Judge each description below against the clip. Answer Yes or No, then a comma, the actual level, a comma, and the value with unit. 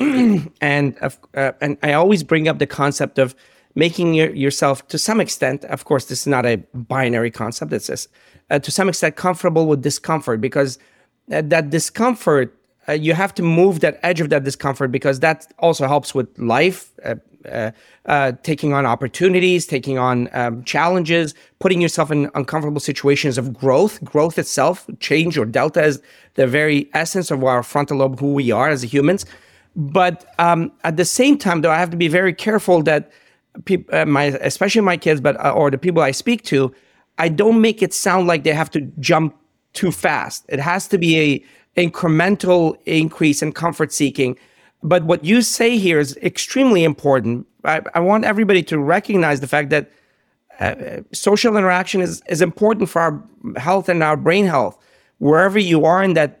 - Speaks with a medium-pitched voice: Yes, medium, 160 Hz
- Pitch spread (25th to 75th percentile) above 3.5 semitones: Yes, average, 4.2 semitones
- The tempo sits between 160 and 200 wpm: Yes, average, 185 wpm